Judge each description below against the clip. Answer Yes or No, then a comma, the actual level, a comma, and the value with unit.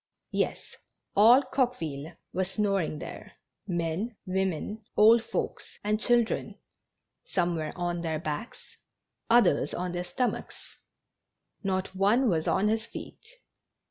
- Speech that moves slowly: Yes, slow, 120 wpm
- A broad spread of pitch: No, average, 4.7 semitones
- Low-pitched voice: No, high, 195 Hz